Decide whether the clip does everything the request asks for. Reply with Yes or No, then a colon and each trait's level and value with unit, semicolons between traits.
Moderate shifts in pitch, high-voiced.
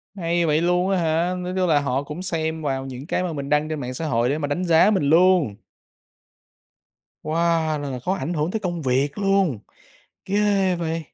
No: average, 3.9 semitones; medium, 165 Hz